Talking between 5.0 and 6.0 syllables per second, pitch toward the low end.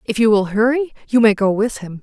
No: 5.7 syllables/s; high, 220 Hz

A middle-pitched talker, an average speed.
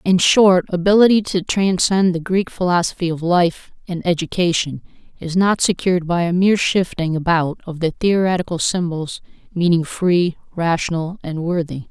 Yes: medium, 175 Hz; average, 145 wpm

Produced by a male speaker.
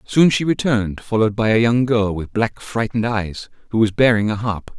Yes: male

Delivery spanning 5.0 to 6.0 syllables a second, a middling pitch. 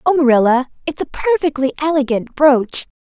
No: 5.2 syllables/s; very high, 280 Hz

